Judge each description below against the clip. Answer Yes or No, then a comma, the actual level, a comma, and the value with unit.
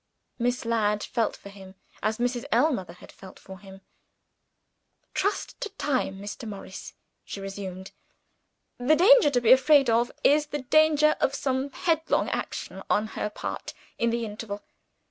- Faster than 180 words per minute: No, average, 150 wpm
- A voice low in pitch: No, high, 235 Hz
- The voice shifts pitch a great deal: Yes, wide, 5.9 semitones